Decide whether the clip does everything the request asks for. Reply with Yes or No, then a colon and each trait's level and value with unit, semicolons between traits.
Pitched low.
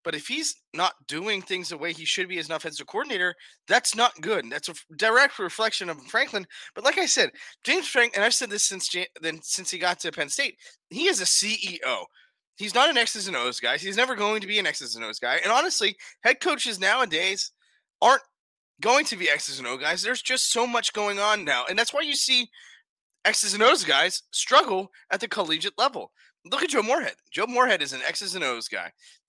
No: high, 205 Hz